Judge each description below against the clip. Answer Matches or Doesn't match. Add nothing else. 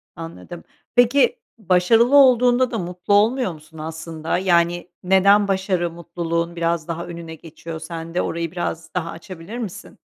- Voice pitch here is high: Doesn't match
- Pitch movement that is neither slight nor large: Matches